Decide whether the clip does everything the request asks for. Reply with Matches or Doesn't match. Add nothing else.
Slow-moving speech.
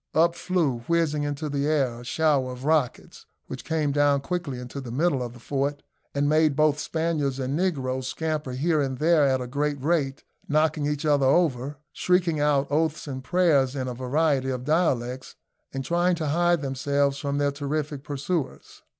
Doesn't match